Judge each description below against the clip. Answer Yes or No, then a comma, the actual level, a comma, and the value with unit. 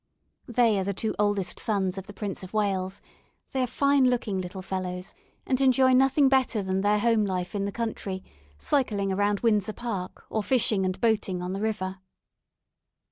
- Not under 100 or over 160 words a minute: No, average, 180 wpm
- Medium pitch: No, high, 205 Hz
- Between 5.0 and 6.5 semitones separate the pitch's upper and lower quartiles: No, average, 3.8 semitones